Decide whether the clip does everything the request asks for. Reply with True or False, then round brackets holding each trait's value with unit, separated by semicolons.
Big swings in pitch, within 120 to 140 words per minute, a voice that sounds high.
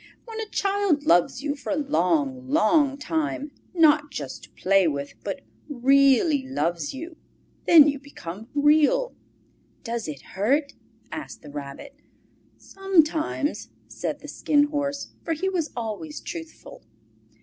True (6.8 semitones; 135 wpm; 285 Hz)